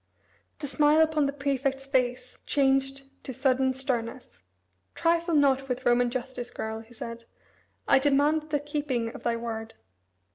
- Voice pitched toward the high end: Yes, very high, 270 Hz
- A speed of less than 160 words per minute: Yes, average, 145 wpm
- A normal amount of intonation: Yes, average, 3.0 semitones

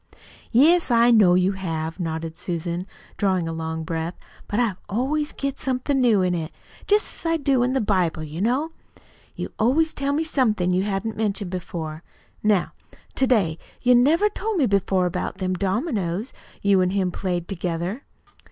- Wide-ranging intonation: Yes, wide, 6.3 semitones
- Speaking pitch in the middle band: No, high, 200 Hz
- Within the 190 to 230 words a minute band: No, average, 170 wpm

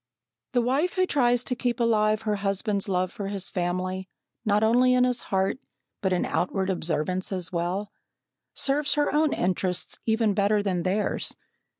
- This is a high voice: Yes, high, 205 Hz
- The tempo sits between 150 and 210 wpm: Yes, average, 165 wpm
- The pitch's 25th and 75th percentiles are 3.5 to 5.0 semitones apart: Yes, average, 4.5 semitones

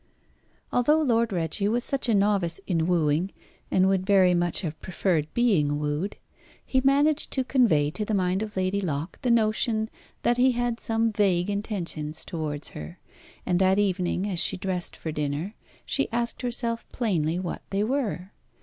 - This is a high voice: Yes, high, 195 Hz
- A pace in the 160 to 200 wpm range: Yes, average, 170 wpm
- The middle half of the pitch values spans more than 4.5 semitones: Yes, average, 5.2 semitones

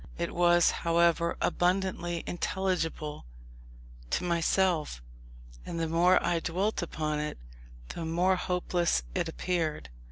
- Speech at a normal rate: No, slow, 115 wpm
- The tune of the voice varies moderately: No, narrow, 1.7 semitones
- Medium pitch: Yes, medium, 170 Hz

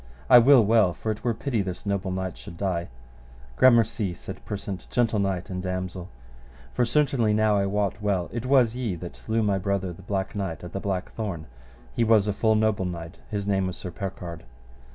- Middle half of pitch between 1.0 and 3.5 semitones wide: Yes, average, 3.2 semitones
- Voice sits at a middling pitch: No, low, 100 Hz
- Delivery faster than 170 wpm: Yes, average, 200 wpm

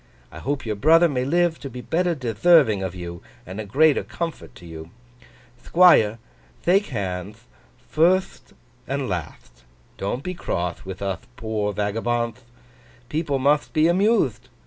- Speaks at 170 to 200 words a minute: No, average, 145 wpm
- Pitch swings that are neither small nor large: No, wide, 8.3 semitones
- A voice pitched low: Yes, low, 125 Hz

